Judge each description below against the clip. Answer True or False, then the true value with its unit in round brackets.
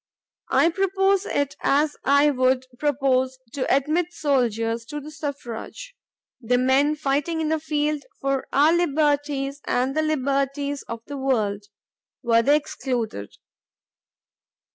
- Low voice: False (280 Hz)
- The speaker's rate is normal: False (125 wpm)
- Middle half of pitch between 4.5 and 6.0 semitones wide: False (2.8 semitones)